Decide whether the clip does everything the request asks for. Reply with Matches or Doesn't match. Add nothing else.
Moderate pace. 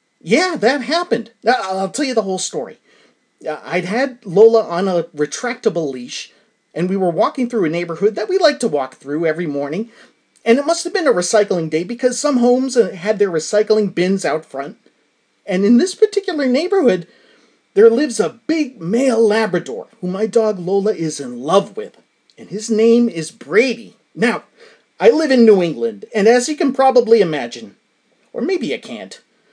Matches